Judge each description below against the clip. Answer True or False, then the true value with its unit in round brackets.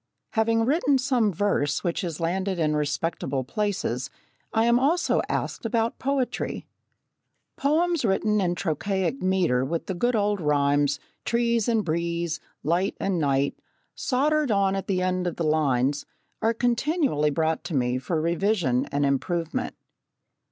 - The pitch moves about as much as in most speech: False (7.0 semitones)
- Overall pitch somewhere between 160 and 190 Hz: True (185 Hz)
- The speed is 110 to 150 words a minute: True (145 wpm)